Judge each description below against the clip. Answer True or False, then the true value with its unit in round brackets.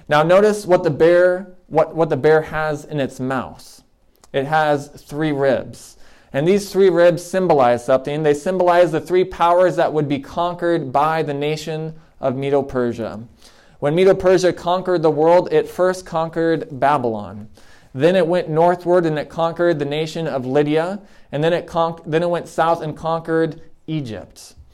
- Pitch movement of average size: True (3.1 semitones)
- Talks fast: False (170 wpm)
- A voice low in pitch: False (160 Hz)